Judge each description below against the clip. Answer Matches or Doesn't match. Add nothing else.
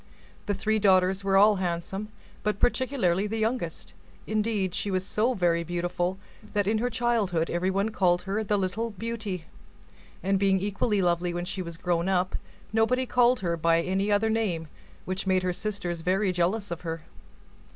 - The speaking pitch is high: Matches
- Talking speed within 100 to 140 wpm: Doesn't match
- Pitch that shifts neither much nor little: Matches